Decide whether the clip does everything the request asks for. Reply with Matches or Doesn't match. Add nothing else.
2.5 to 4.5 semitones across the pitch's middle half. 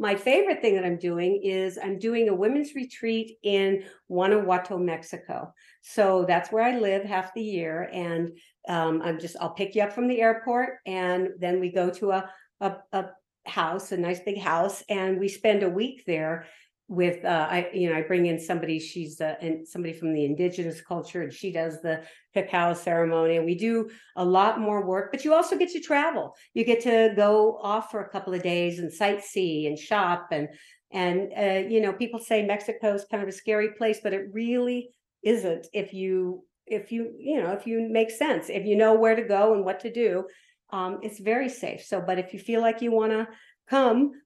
Matches